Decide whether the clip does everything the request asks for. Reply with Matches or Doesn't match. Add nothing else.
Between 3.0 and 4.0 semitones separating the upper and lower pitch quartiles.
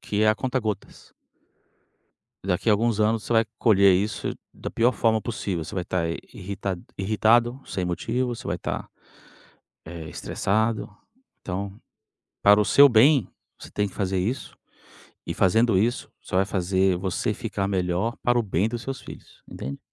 Matches